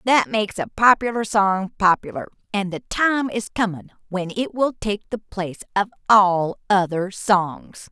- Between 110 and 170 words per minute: Yes, average, 160 wpm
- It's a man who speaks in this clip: No, female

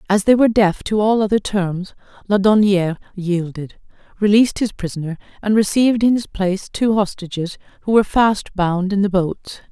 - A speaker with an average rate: Yes, average, 165 wpm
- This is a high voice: Yes, high, 200 Hz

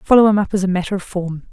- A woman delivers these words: Yes, female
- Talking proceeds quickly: Yes, fast, 315 wpm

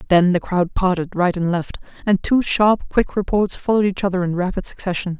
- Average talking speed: No, fast, 210 wpm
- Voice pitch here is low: No, medium, 185 Hz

